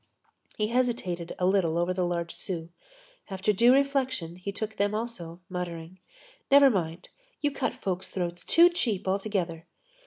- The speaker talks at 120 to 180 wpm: Yes, average, 150 wpm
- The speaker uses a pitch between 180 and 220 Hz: Yes, high, 190 Hz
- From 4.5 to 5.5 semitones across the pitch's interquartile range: Yes, average, 5.2 semitones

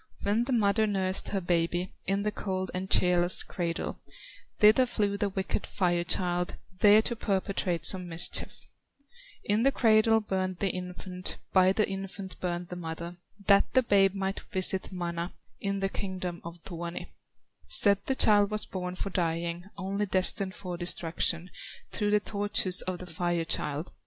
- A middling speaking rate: Yes, average, 160 wpm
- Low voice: No, medium, 185 Hz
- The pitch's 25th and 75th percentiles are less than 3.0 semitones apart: Yes, narrow, 2.4 semitones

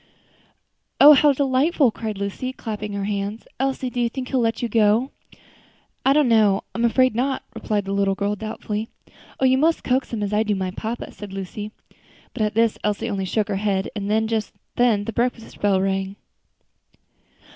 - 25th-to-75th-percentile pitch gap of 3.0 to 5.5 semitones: Yes, average, 3.7 semitones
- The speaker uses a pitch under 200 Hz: No, high, 220 Hz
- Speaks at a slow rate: No, average, 185 wpm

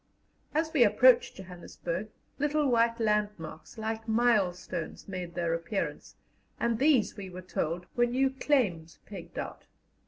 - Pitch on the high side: Yes, high, 210 Hz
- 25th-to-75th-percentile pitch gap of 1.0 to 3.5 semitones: No, average, 5.2 semitones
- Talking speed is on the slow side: Yes, slow, 130 wpm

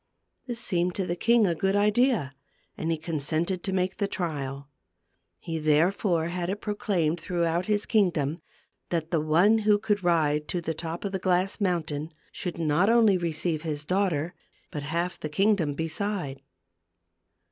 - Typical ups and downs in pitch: Yes, average, 3.9 semitones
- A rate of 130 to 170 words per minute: Yes, average, 160 wpm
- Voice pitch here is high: No, medium, 175 Hz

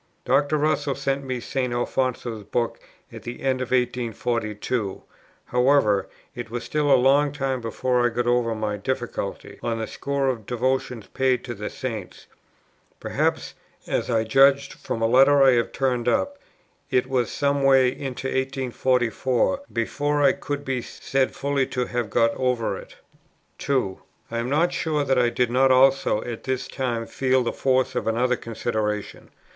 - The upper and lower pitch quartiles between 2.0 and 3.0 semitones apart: Yes, narrow, 2.5 semitones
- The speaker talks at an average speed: Yes, average, 165 wpm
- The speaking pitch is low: Yes, low, 125 Hz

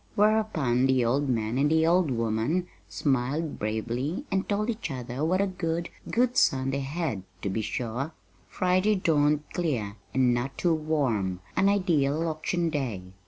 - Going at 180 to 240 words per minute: No, average, 160 wpm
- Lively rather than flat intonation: Yes, wide, 6.3 semitones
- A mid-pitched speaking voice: Yes, medium, 145 Hz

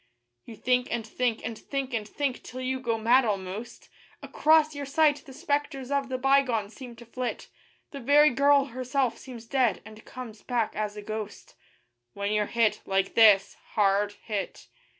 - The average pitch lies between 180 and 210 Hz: No, high, 240 Hz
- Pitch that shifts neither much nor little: Yes, average, 3.9 semitones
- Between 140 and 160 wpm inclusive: No, average, 170 wpm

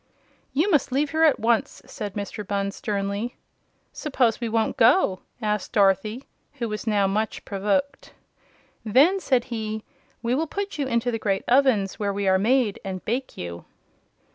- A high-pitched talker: Yes, high, 225 Hz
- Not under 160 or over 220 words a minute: Yes, average, 165 wpm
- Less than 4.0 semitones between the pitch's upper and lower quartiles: No, average, 4.7 semitones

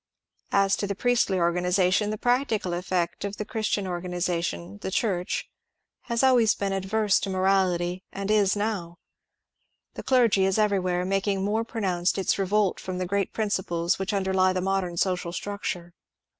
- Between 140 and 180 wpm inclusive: Yes, average, 155 wpm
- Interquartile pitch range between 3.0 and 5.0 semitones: No, narrow, 2.4 semitones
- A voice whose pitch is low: No, high, 195 Hz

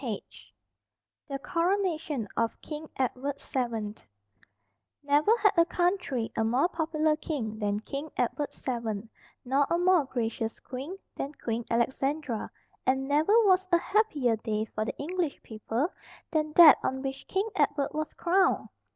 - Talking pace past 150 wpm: No, average, 140 wpm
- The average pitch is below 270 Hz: No, very high, 285 Hz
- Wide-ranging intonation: Yes, wide, 5.9 semitones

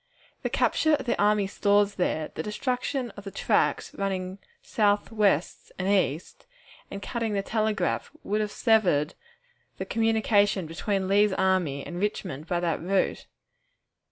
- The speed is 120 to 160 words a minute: Yes, average, 145 wpm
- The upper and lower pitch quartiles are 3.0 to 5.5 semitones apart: No, narrow, 2.6 semitones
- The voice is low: No, high, 200 Hz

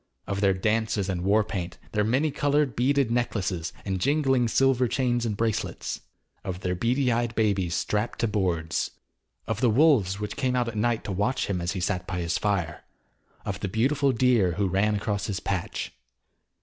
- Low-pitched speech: Yes, low, 105 Hz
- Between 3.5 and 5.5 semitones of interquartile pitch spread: Yes, average, 4.3 semitones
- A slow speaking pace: No, average, 185 wpm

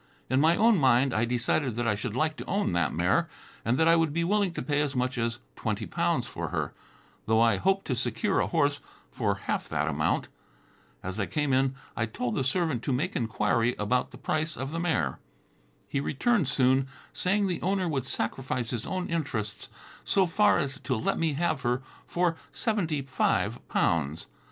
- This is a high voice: No, low, 135 Hz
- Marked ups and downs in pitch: Yes, wide, 6.2 semitones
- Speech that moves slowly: No, average, 195 wpm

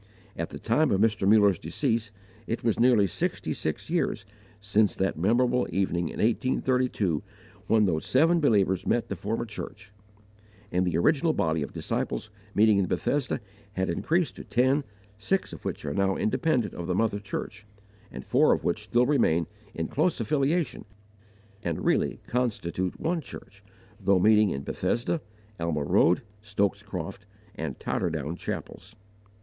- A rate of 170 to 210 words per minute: No, average, 155 wpm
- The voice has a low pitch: Yes, low, 105 Hz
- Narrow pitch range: No, average, 5.1 semitones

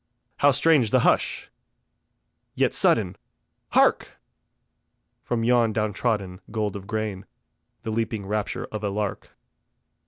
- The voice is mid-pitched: No, low, 110 Hz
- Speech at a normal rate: No, slow, 120 wpm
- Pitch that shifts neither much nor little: No, narrow, 2.1 semitones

